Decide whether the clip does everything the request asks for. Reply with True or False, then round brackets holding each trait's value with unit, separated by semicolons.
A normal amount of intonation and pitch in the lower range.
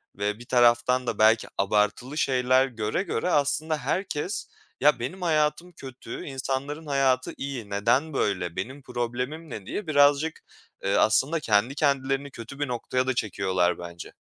True (4.1 semitones; 130 Hz)